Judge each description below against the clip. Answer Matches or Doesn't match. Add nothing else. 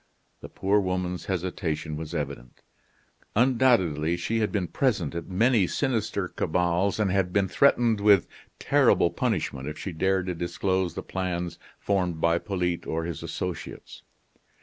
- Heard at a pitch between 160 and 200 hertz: Doesn't match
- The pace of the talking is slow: Doesn't match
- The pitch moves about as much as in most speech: Matches